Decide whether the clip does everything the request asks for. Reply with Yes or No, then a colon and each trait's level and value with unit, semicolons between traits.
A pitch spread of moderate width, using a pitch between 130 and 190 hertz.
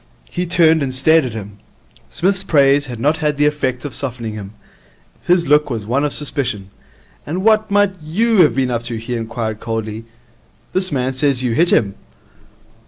No: wide, 5.7 semitones; medium, 140 Hz